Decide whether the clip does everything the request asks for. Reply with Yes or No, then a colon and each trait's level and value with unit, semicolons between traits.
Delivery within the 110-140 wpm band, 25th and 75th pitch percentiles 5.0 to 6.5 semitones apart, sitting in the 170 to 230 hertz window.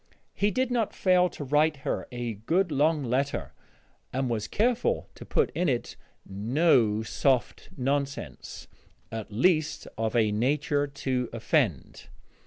No: slow, 135 wpm; wide, 5.6 semitones; medium, 140 Hz